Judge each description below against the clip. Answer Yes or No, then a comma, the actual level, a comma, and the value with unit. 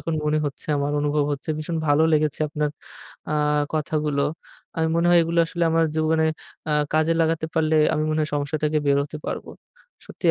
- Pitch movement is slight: Yes, narrow, 1.4 semitones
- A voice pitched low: No, medium, 155 Hz